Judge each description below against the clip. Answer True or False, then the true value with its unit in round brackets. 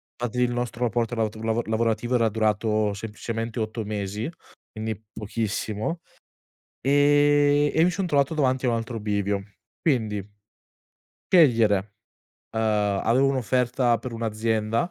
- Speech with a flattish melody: False (3.0 semitones)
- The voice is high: False (115 Hz)